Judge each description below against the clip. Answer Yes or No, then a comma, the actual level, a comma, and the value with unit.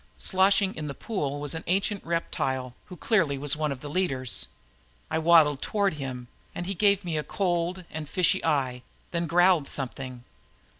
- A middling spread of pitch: Yes, average, 4.9 semitones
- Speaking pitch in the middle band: Yes, medium, 160 Hz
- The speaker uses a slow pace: No, average, 170 wpm